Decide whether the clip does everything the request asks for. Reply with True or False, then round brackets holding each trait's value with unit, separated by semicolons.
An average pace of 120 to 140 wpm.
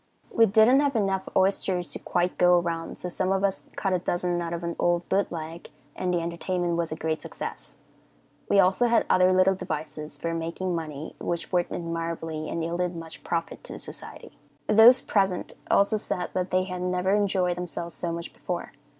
False (195 wpm)